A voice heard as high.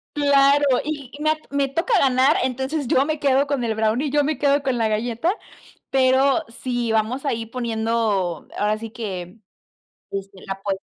Yes: very high, 255 Hz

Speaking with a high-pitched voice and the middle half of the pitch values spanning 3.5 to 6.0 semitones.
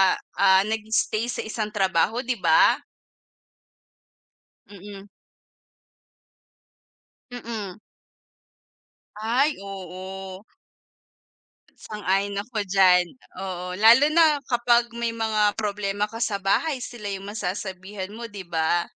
No: high, 205 Hz; average, 3.0 semitones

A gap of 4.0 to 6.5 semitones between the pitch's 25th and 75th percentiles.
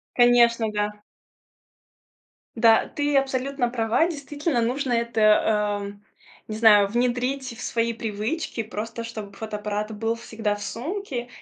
No: average, 2.8 semitones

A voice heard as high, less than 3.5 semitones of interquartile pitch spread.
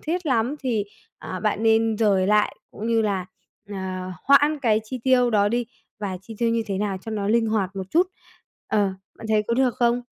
Yes: high, 220 Hz; average, 3.0 semitones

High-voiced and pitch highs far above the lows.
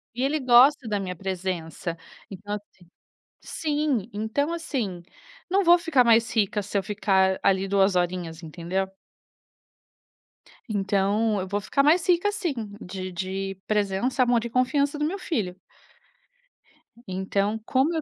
Yes: high, 210 Hz; wide, 6.2 semitones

